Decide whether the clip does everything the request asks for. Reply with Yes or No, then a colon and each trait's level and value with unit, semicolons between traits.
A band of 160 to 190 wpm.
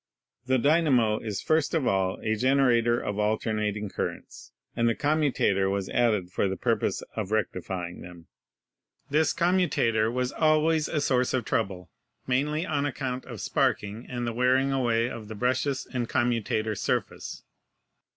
No: average, 150 wpm